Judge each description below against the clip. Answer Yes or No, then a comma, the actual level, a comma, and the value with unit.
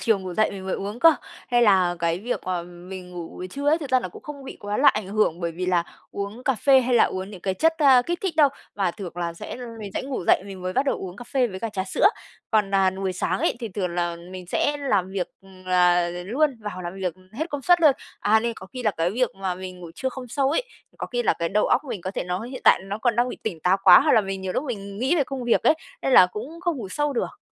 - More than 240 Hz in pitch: No, high, 205 Hz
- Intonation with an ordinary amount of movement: No, wide, 5.8 semitones